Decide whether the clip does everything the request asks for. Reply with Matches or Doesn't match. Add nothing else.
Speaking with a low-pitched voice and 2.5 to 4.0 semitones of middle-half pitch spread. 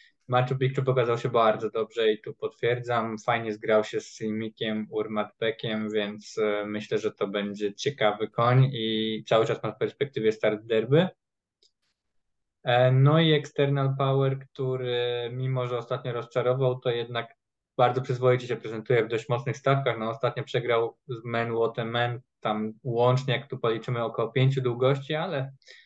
Matches